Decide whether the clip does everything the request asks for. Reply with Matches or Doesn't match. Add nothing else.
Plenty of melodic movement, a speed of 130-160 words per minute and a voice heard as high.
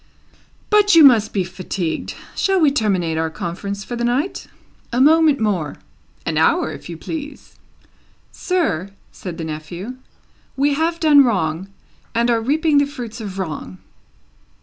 Matches